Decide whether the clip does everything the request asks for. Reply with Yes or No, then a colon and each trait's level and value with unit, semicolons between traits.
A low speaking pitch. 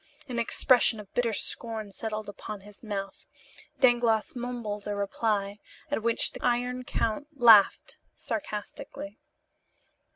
No: high, 220 Hz